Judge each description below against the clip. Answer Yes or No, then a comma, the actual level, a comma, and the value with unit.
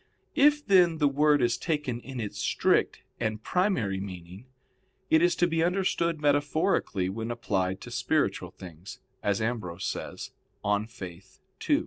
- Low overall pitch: Yes, low, 120 Hz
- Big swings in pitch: Yes, wide, 8.4 semitones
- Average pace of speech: Yes, average, 145 wpm